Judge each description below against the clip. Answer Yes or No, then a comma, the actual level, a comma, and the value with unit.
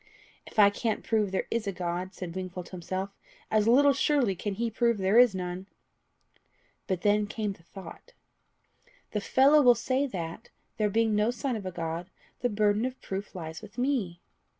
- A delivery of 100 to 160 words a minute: No, average, 185 wpm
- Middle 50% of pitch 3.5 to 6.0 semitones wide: Yes, average, 4.0 semitones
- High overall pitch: Yes, high, 205 Hz